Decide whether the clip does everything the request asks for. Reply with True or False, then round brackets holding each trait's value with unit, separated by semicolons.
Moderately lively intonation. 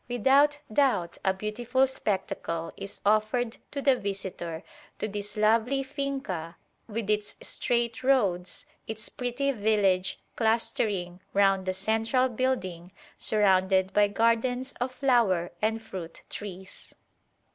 True (4.5 semitones)